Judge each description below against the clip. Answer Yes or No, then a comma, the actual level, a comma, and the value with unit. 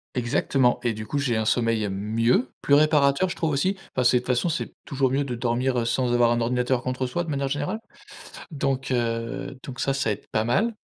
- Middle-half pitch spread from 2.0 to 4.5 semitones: Yes, average, 2.8 semitones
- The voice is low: Yes, low, 125 Hz